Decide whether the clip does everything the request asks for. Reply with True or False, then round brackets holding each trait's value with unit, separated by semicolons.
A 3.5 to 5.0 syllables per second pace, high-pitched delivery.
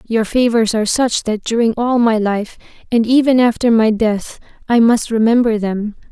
True (4.8 syllables/s; 225 Hz)